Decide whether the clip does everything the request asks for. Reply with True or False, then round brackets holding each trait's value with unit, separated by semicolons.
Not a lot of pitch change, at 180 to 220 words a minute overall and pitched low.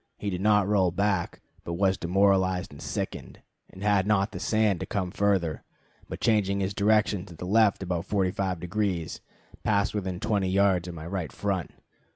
True (2.1 semitones; 185 wpm; 95 Hz)